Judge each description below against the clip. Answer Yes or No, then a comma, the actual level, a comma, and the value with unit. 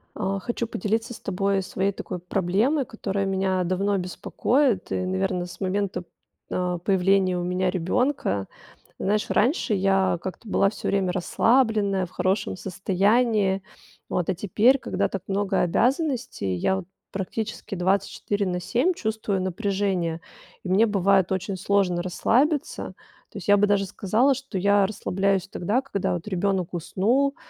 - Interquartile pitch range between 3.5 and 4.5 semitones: No, narrow, 2.6 semitones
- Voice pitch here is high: Yes, high, 195 Hz